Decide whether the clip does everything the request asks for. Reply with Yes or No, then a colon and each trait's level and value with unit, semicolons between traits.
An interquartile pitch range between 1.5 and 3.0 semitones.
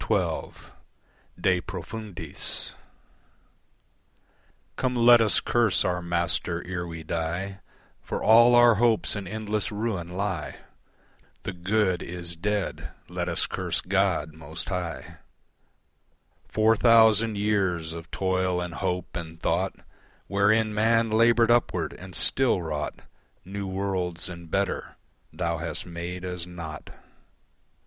No: average, 3.9 semitones